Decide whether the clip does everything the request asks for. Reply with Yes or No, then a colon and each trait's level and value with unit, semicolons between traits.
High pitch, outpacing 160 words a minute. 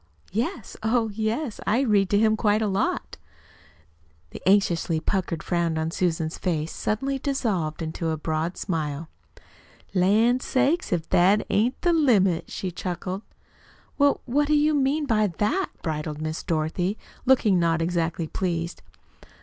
No: high, 195 Hz; average, 140 wpm